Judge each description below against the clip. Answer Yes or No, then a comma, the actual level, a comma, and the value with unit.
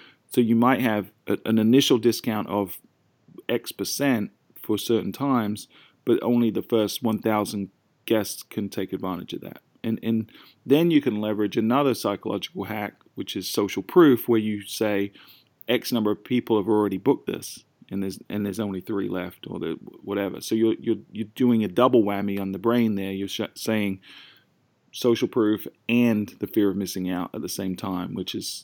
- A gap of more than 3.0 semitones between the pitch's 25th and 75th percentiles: No, average, 2.7 semitones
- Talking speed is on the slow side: No, average, 185 wpm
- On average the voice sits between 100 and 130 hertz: Yes, low, 110 Hz